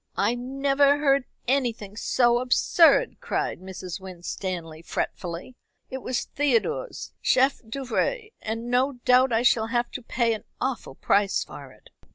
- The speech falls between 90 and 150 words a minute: Yes, average, 140 wpm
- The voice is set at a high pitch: Yes, high, 245 Hz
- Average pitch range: Yes, average, 4.6 semitones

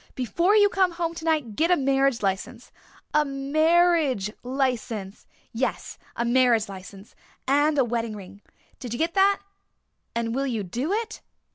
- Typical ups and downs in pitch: No, wide, 6.2 semitones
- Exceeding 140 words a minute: Yes, average, 150 wpm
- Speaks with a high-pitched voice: Yes, very high, 265 Hz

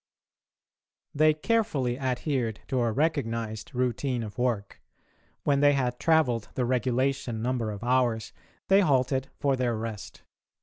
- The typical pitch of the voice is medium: No, low, 125 Hz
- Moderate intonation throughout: Yes, average, 3.1 semitones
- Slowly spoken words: Yes, slow, 130 wpm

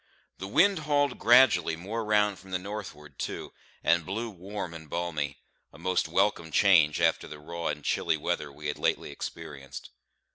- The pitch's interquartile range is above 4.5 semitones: Yes, average, 5.2 semitones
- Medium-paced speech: Yes, average, 170 wpm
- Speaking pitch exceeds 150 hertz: No, very low, 90 Hz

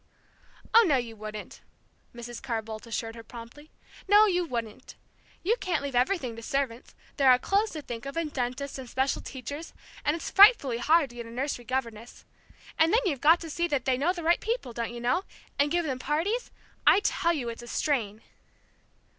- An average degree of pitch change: No, wide, 5.8 semitones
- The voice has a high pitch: Yes, very high, 270 Hz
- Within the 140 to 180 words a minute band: No, average, 200 wpm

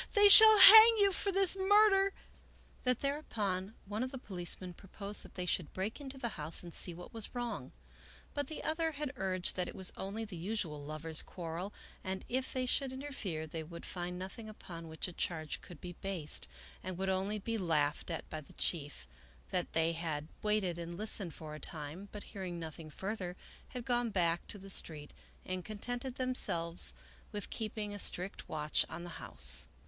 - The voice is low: No, high, 190 Hz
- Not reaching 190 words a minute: No, average, 195 wpm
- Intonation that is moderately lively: No, wide, 6.4 semitones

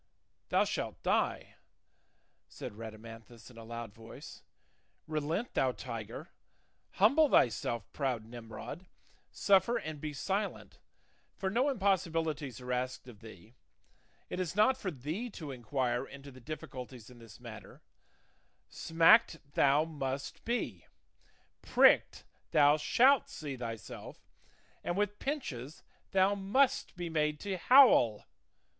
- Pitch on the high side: No, medium, 145 Hz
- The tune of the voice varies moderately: No, wide, 7.9 semitones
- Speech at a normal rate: No, slow, 125 wpm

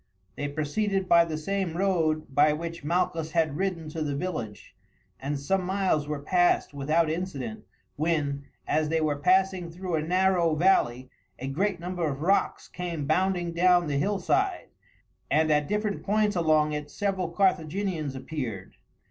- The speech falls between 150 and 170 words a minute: Yes, average, 155 wpm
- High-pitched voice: No, medium, 165 Hz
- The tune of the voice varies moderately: Yes, average, 3.8 semitones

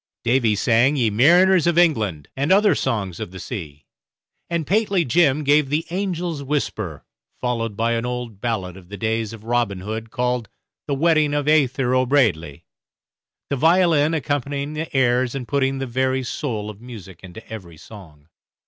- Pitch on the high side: No, low, 125 Hz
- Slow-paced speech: No, average, 165 wpm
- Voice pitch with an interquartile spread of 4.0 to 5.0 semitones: No, wide, 5.4 semitones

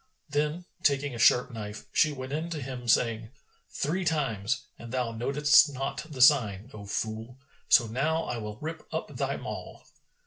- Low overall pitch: Yes, low, 130 Hz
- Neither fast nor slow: Yes, average, 170 wpm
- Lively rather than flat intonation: No, average, 4.6 semitones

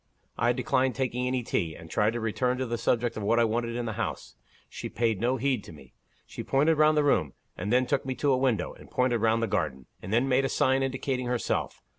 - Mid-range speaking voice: No, low, 120 Hz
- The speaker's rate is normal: No, fast, 245 wpm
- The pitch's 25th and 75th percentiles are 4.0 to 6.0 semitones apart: No, average, 2.7 semitones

